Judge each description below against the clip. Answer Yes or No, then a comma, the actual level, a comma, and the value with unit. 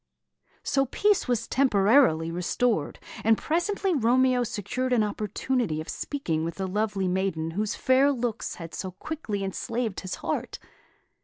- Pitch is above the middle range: Yes, high, 220 Hz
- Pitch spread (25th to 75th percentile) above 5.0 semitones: Yes, wide, 5.5 semitones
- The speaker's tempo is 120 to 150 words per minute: Yes, average, 140 wpm